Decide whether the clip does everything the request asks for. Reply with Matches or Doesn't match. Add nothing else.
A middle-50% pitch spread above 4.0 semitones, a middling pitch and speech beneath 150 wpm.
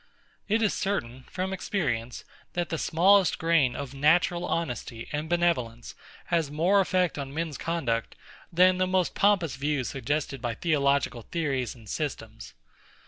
Matches